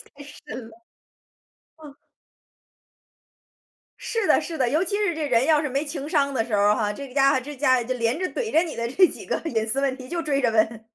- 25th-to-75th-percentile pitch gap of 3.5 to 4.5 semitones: No, average, 5.0 semitones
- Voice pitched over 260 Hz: Yes, very high, 275 Hz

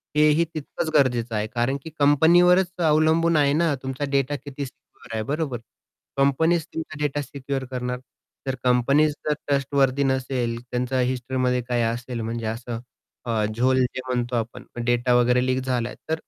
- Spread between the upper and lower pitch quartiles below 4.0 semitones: Yes, average, 3.0 semitones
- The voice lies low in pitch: Yes, low, 130 Hz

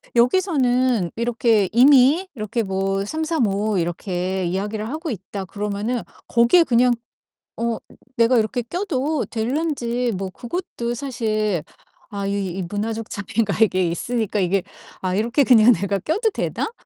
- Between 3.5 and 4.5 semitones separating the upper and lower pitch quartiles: Yes, average, 4.1 semitones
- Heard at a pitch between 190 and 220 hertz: No, high, 230 Hz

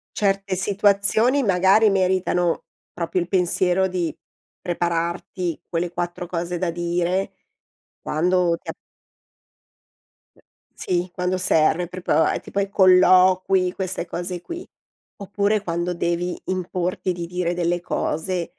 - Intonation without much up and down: Yes, narrow, 1.6 semitones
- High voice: No, medium, 180 Hz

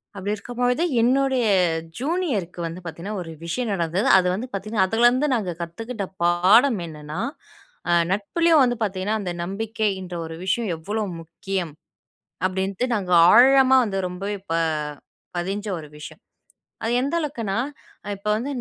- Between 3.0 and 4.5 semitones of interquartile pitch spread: No, average, 5.0 semitones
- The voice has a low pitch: No, high, 205 Hz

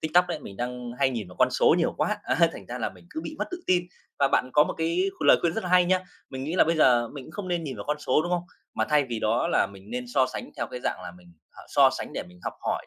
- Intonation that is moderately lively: No, wide, 6.1 semitones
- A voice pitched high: No, medium, 140 Hz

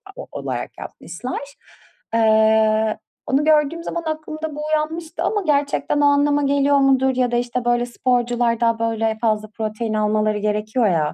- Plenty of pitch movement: No, average, 4.7 semitones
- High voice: Yes, high, 245 Hz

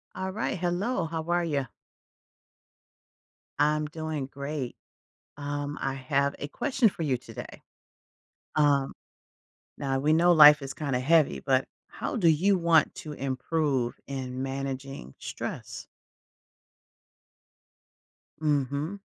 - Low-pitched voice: No, medium, 145 Hz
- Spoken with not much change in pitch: No, average, 3.2 semitones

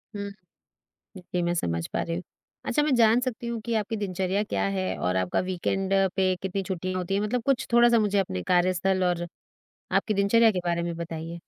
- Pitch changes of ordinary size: Yes, average, 3.9 semitones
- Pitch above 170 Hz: Yes, high, 190 Hz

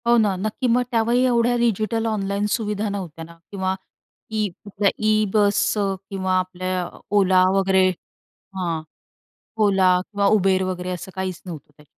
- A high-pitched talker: Yes, high, 195 Hz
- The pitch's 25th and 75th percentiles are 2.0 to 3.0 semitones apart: Yes, narrow, 2.6 semitones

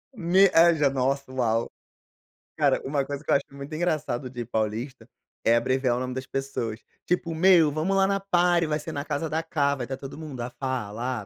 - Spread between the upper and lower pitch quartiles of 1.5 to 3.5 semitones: No, average, 4.1 semitones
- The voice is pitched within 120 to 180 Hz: Yes, medium, 140 Hz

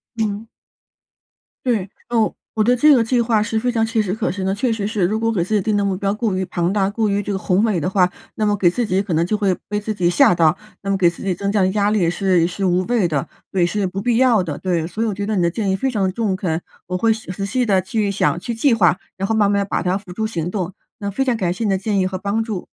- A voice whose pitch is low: No, high, 200 Hz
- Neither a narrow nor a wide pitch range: Yes, average, 3.1 semitones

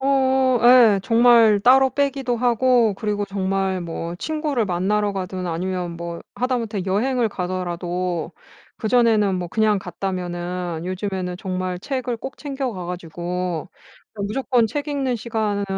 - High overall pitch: Yes, high, 205 Hz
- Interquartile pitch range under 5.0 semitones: No, average, 5.3 semitones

